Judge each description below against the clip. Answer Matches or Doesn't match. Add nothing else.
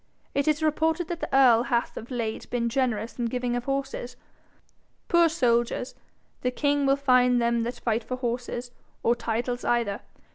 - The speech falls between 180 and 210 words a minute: Doesn't match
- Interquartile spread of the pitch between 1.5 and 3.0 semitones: Matches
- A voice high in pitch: Matches